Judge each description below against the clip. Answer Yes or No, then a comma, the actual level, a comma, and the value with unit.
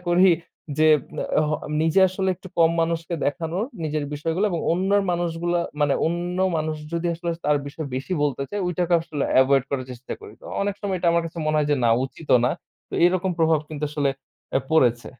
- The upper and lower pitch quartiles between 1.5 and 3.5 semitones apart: Yes, average, 3.0 semitones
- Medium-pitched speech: Yes, medium, 165 Hz